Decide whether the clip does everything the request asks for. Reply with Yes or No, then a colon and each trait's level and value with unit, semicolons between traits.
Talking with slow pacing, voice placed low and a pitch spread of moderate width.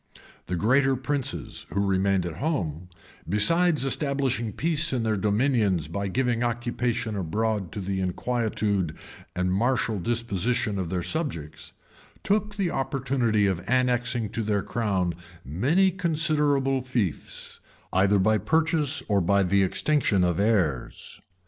No: slow, 130 wpm; low, 115 Hz; wide, 5.8 semitones